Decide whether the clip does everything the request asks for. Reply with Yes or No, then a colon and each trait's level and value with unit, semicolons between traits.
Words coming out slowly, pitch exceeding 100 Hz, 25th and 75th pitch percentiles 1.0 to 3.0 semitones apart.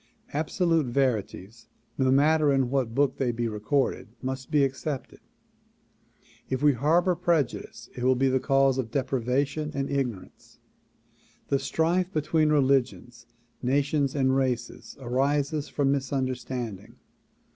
Yes: slow, 125 wpm; low, 135 Hz; narrow, 2.5 semitones